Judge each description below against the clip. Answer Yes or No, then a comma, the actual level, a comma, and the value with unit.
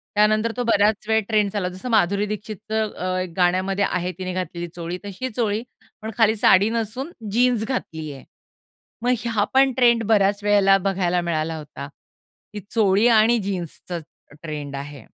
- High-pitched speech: Yes, high, 205 Hz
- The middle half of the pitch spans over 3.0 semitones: Yes, average, 3.6 semitones